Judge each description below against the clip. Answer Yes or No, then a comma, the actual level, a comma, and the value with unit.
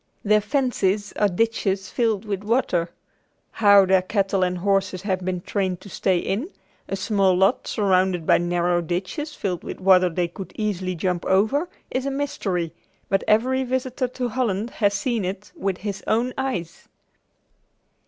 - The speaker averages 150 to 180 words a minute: Yes, average, 165 wpm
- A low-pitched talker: No, high, 195 Hz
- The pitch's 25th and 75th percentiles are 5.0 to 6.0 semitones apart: No, average, 3.6 semitones